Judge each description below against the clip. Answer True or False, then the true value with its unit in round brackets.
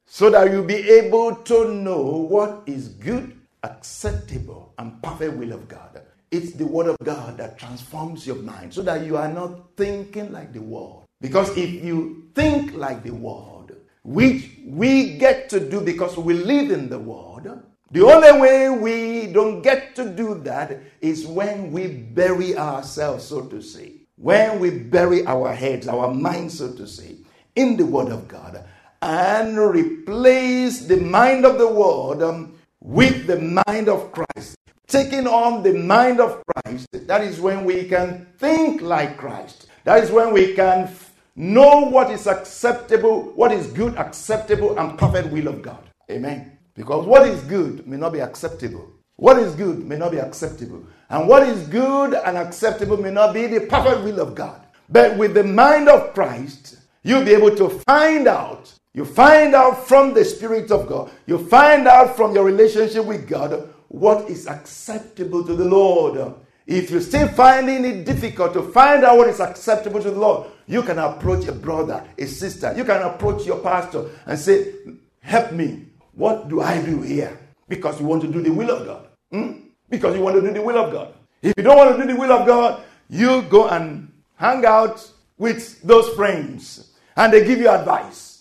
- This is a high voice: True (200 Hz)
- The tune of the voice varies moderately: False (7.0 semitones)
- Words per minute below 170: False (185 wpm)